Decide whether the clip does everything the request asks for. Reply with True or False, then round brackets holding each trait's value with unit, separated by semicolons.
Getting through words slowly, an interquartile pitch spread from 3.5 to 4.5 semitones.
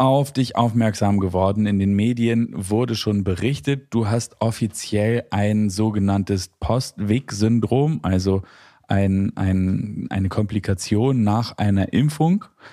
False (115 wpm; 2.9 semitones)